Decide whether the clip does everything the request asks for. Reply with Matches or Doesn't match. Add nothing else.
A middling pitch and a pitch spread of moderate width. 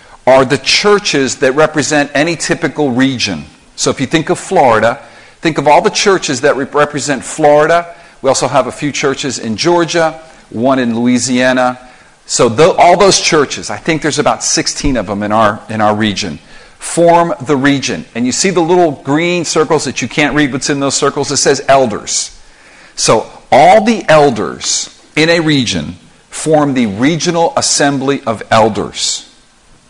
Matches